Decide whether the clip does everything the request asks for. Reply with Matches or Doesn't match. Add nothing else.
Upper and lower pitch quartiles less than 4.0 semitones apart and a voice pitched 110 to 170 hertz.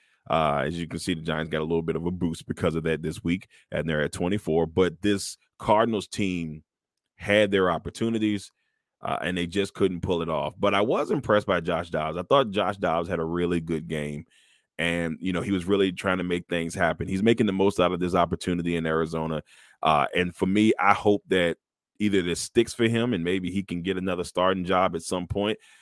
Doesn't match